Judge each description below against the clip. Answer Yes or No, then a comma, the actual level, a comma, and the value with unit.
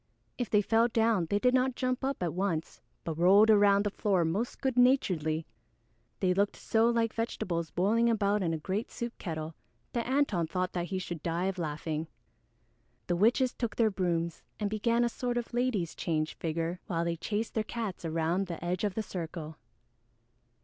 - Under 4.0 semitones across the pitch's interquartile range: No, average, 5.3 semitones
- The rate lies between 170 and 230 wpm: Yes, average, 185 wpm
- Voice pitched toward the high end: Yes, high, 195 Hz